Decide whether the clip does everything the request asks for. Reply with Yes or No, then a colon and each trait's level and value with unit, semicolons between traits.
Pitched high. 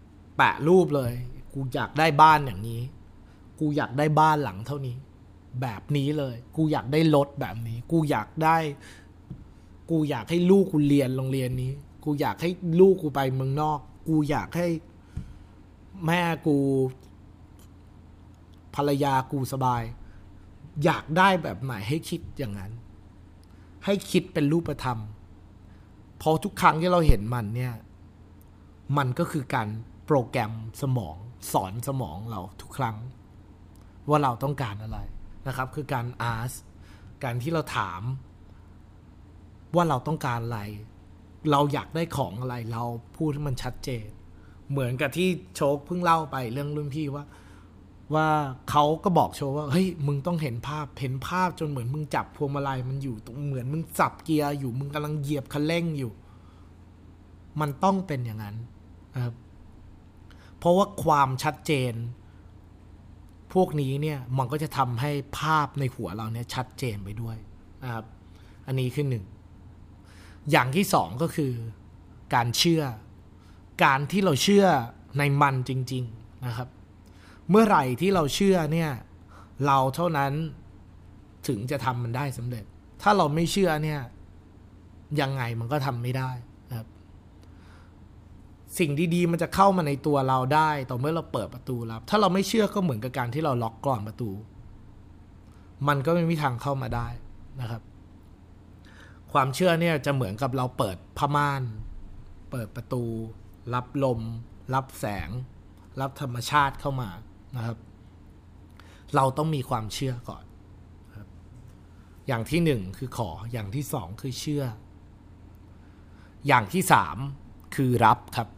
No: low, 125 Hz